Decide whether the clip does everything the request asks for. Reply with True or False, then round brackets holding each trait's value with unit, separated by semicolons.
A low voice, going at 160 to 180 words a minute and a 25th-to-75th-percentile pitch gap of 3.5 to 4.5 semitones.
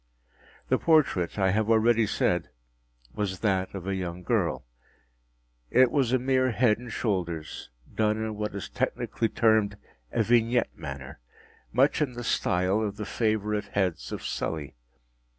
False (105 Hz; 150 wpm; 3.8 semitones)